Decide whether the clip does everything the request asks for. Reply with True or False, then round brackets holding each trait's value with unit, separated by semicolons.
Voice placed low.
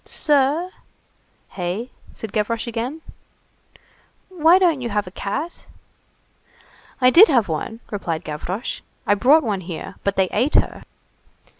False (230 Hz)